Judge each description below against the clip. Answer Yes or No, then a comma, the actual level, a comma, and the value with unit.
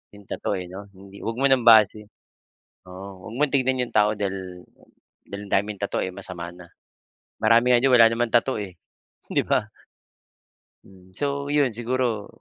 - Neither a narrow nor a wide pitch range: Yes, average, 4.2 semitones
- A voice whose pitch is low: Yes, low, 105 Hz